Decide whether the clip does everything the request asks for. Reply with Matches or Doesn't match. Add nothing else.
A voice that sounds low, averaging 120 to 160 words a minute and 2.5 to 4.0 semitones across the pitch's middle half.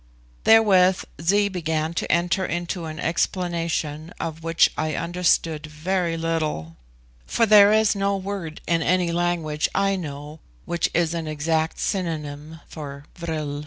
Doesn't match